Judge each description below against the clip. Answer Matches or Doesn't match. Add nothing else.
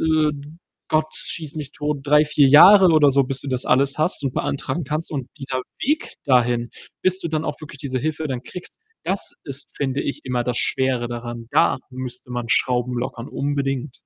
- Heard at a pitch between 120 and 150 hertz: Matches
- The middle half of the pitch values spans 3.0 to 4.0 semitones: Matches